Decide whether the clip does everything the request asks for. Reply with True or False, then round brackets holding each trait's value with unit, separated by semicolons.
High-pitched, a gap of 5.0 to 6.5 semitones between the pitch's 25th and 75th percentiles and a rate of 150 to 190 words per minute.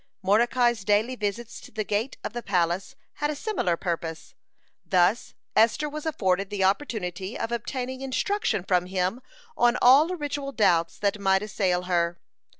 True (210 Hz; 5.3 semitones; 155 wpm)